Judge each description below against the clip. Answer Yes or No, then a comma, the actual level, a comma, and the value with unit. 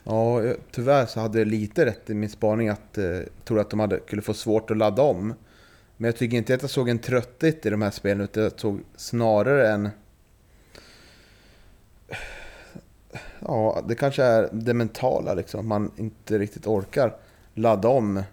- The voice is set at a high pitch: No, low, 110 Hz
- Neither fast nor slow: Yes, average, 175 wpm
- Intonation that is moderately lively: No, narrow, 2.0 semitones